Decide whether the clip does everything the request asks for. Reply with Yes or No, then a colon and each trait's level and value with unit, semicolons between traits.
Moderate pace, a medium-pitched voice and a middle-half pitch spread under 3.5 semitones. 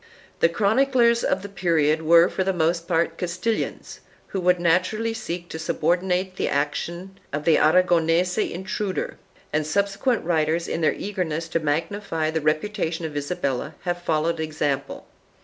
Yes: average, 150 wpm; medium, 170 Hz; average, 3.1 semitones